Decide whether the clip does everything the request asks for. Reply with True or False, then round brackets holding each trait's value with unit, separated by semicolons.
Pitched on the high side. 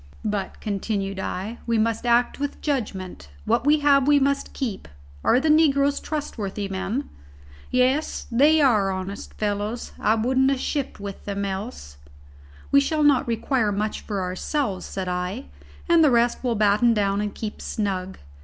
True (225 Hz)